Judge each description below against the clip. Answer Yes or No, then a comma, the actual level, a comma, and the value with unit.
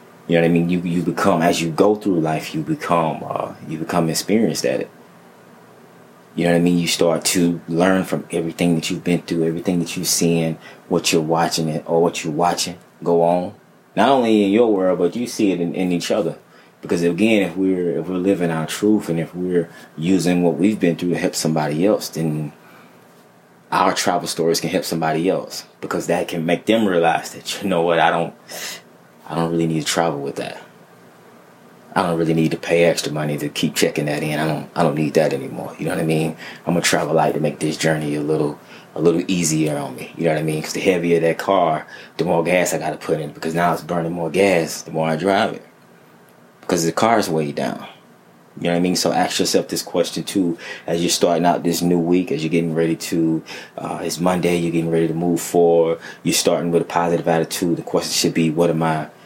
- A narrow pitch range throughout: Yes, narrow, 1.4 semitones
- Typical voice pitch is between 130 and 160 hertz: No, very low, 85 Hz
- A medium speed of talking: No, fast, 235 wpm